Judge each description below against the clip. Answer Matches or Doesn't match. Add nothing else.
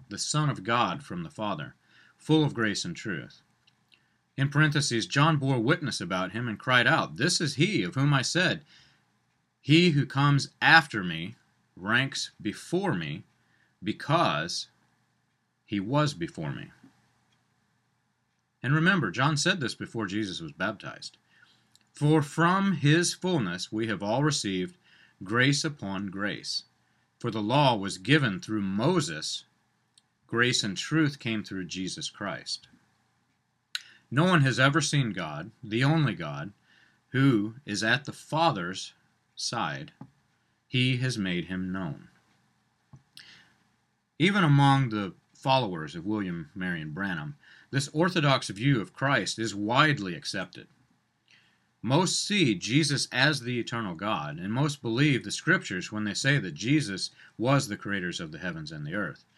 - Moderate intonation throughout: Doesn't match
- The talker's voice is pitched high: Doesn't match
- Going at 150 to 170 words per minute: Doesn't match